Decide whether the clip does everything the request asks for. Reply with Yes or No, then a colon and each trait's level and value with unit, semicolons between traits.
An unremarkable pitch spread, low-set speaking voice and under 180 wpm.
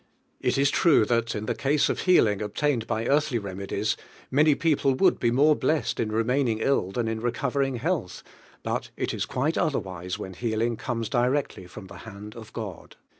No: average, 4.6 semitones; low, 120 Hz; average, 185 wpm